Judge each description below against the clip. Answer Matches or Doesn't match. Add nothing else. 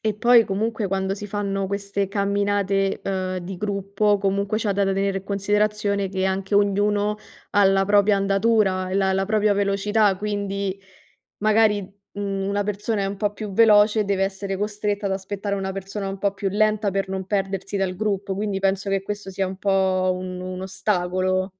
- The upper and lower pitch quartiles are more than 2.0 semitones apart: Doesn't match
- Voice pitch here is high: Matches